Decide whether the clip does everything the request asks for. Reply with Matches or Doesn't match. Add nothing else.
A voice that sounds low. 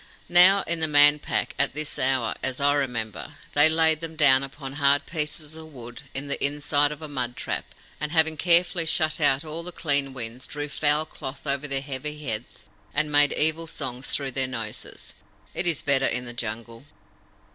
Doesn't match